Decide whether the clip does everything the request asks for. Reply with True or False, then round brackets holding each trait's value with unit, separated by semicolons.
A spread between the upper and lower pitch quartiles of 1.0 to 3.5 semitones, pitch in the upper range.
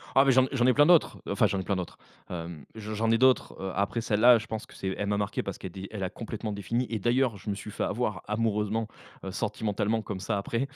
False (2.7 semitones; 110 Hz)